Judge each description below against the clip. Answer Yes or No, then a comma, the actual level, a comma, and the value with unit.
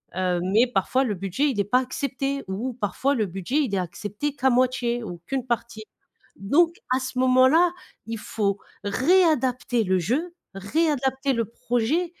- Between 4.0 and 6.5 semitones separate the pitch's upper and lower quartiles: Yes, average, 5.0 semitones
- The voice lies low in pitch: No, very high, 250 Hz